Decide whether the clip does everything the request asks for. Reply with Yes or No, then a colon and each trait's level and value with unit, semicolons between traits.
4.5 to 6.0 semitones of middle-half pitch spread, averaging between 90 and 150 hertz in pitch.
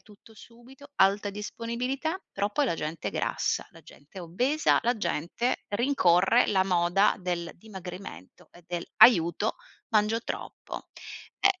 No: average, 5.3 semitones; high, 205 Hz